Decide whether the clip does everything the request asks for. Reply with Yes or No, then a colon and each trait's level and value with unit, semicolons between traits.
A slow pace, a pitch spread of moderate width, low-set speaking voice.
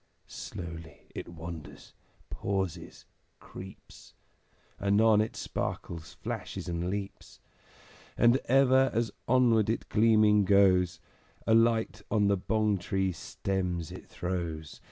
Yes: slow, 110 wpm; average, 4.2 semitones; low, 100 Hz